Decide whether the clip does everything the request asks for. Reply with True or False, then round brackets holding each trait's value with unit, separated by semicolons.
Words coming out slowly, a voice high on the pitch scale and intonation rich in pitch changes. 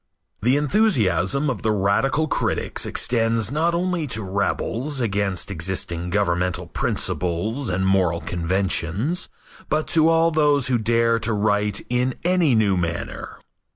False (130 wpm; 110 Hz; 7.1 semitones)